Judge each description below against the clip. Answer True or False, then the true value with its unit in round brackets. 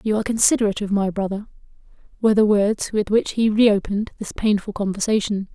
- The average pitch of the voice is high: True (210 Hz)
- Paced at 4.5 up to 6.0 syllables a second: False (6.6 syllables/s)